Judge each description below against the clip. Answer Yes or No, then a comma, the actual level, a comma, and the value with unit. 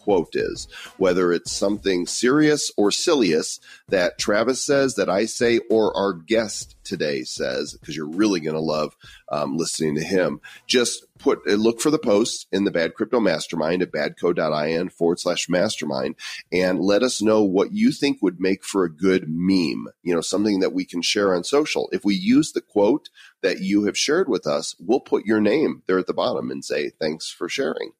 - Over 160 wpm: Yes, average, 195 wpm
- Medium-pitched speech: No, low, 105 Hz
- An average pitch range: No, wide, 7.4 semitones